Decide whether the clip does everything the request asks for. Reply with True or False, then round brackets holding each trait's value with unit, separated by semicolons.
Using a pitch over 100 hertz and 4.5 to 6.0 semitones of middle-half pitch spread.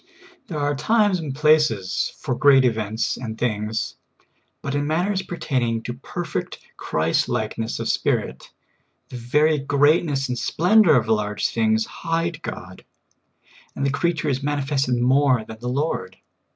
True (135 Hz; 5.3 semitones)